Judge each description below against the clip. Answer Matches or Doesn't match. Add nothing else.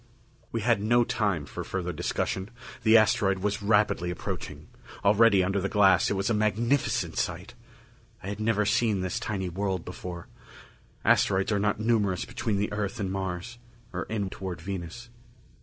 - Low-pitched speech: Matches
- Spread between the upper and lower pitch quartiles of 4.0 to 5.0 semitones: Doesn't match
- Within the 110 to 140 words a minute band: Doesn't match